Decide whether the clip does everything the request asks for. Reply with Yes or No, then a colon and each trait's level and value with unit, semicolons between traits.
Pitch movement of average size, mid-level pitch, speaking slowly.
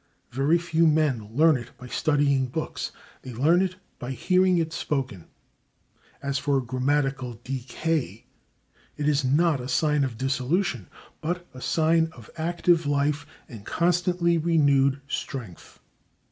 Yes: average, 4.1 semitones; medium, 145 Hz; slow, 130 wpm